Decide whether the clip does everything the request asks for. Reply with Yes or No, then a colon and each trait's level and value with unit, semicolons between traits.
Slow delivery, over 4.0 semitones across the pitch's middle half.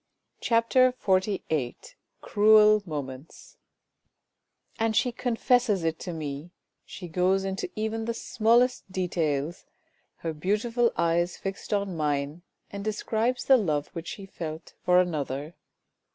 Yes: slow, 125 wpm; wide, 5.4 semitones